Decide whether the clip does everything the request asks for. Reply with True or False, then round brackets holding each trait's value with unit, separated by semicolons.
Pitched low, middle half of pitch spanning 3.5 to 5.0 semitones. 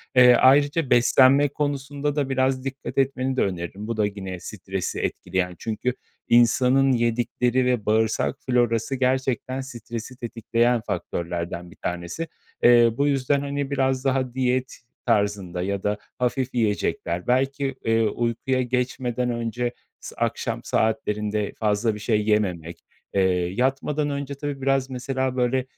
True (125 Hz; 3.8 semitones)